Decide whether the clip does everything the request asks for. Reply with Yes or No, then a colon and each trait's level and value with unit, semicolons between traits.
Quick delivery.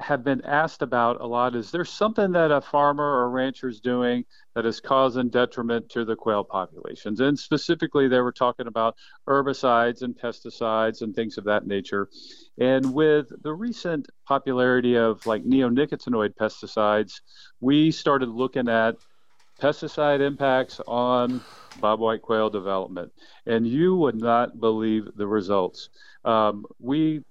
No: average, 150 wpm